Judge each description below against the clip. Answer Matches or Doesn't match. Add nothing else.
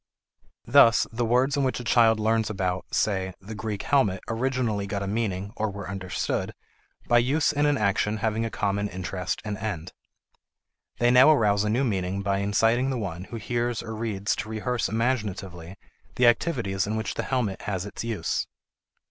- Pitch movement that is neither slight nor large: Matches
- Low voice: Matches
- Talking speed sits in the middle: Matches